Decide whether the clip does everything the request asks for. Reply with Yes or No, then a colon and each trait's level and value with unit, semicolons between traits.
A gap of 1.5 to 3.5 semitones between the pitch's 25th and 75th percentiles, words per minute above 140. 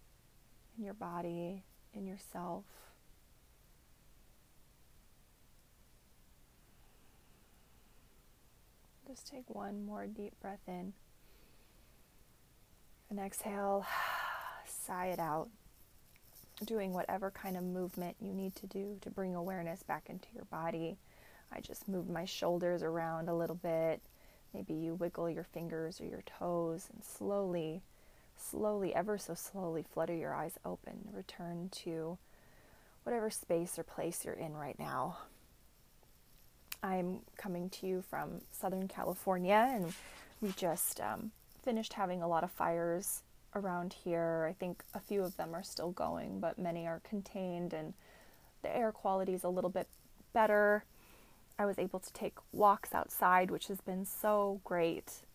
No: average, 3.0 semitones; slow, 135 wpm